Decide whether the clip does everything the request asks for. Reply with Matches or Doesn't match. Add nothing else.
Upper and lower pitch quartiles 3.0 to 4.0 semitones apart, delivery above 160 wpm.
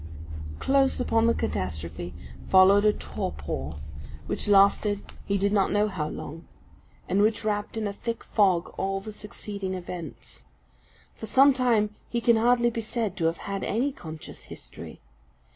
Doesn't match